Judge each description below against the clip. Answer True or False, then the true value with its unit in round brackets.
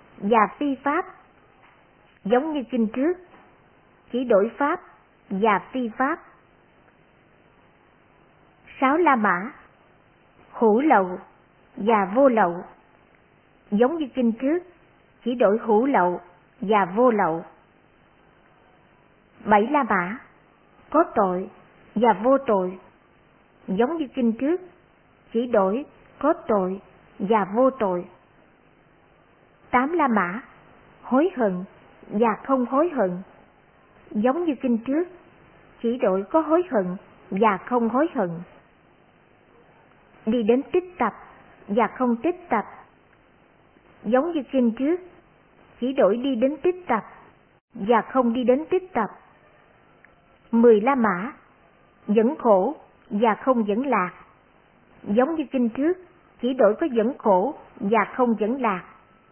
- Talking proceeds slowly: True (120 wpm)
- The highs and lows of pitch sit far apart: False (4.7 semitones)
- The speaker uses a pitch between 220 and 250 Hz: True (240 Hz)